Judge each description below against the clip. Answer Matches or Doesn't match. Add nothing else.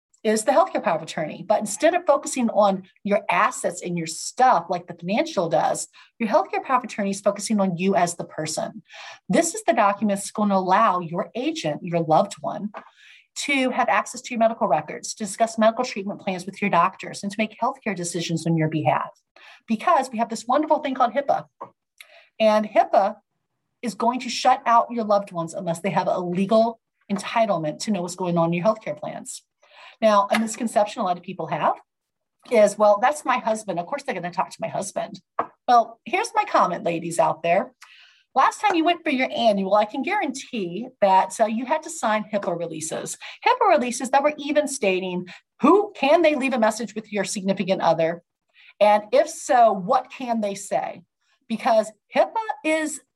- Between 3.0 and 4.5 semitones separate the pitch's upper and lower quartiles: Doesn't match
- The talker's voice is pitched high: Matches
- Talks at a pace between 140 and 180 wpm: Doesn't match